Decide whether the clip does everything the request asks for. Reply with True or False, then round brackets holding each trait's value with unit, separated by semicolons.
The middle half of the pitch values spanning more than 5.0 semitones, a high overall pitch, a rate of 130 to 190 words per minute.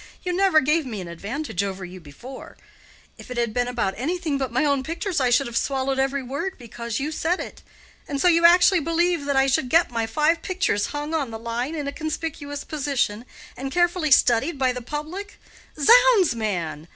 False (5.4 semitones; 275 Hz; 200 wpm)